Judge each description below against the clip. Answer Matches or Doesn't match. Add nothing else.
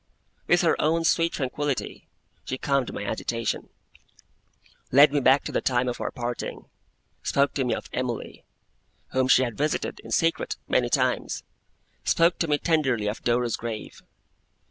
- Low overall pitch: Matches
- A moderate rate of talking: Matches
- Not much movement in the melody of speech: Doesn't match